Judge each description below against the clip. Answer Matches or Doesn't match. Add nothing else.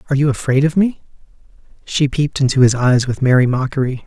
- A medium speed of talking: Matches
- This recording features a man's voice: Matches